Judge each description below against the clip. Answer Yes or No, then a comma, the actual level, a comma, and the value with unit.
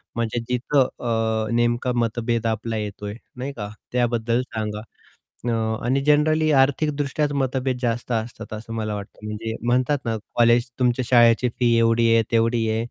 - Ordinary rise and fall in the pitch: No, narrow, 2.1 semitones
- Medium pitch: No, low, 120 Hz